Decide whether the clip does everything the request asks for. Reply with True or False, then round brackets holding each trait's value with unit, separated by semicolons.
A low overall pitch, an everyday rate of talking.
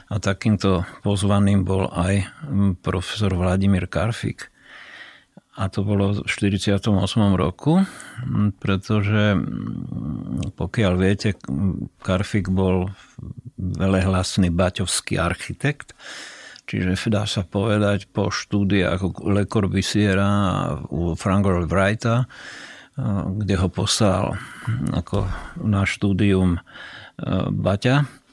False (100 Hz; 85 wpm)